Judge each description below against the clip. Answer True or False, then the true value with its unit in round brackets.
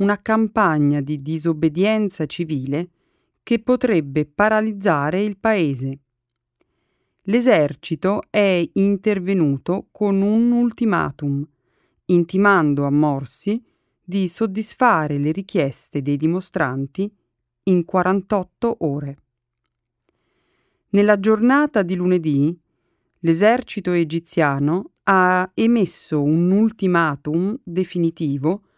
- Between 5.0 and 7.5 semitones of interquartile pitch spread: True (5.3 semitones)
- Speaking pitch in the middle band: True (180 Hz)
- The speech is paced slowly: True (80 wpm)